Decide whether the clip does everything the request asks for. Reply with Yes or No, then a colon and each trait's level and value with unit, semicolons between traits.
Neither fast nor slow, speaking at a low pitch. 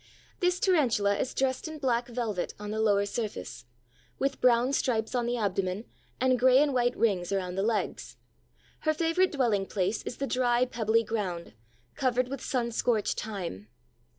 No: average, 165 wpm; high, 235 Hz